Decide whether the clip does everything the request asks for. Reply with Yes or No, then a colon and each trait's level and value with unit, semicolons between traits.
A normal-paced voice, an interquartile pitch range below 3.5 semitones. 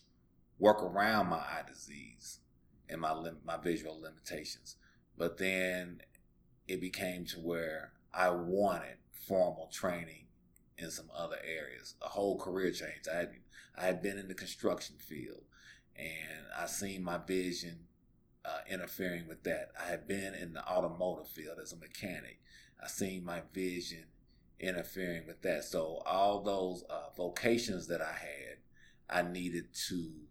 Yes: average, 150 wpm; average, 2.7 semitones